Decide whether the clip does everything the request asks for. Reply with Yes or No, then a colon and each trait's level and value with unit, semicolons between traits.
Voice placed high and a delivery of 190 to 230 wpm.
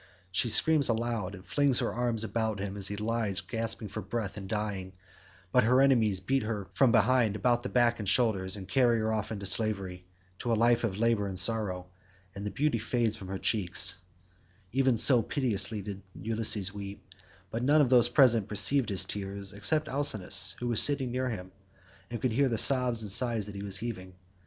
No: low, 110 Hz; average, 195 wpm